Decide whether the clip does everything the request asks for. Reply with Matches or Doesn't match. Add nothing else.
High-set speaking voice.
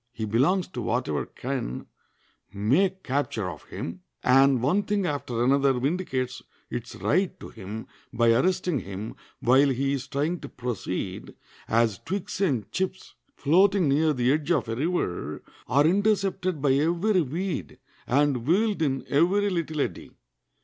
Doesn't match